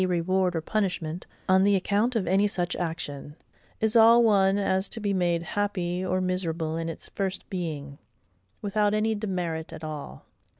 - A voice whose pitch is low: No, medium, 185 Hz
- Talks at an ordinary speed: Yes, average, 165 wpm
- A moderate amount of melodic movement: Yes, average, 3.6 semitones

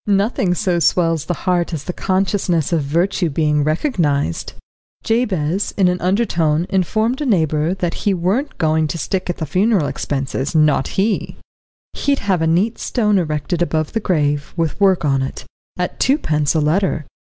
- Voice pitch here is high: No, medium, 175 Hz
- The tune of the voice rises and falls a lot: No, average, 4.2 semitones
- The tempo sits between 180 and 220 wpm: No, average, 165 wpm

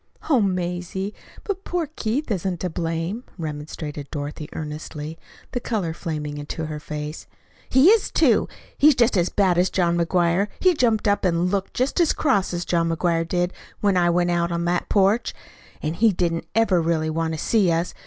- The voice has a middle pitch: Yes, medium, 175 Hz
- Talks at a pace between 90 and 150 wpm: No, average, 185 wpm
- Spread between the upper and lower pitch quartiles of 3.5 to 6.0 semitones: Yes, average, 3.8 semitones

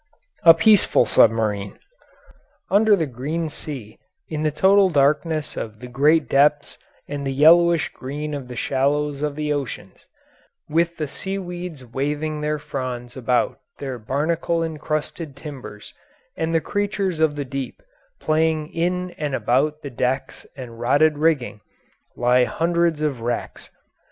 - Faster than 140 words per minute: No, slow, 135 wpm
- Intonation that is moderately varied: Yes, average, 3.6 semitones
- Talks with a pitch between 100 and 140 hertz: No, medium, 150 Hz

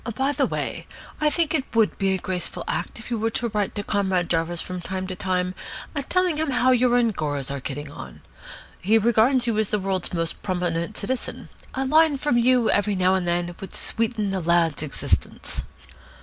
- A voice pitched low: No, high, 200 Hz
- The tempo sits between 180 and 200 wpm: Yes, average, 195 wpm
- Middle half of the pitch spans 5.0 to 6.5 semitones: Yes, wide, 5.4 semitones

